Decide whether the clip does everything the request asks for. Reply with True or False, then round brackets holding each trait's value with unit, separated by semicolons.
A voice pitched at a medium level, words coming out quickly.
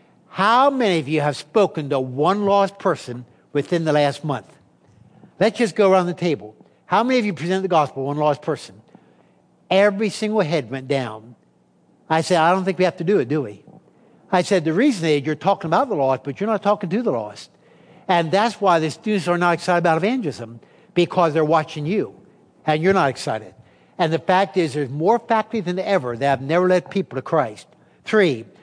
True (175 Hz; 210 wpm)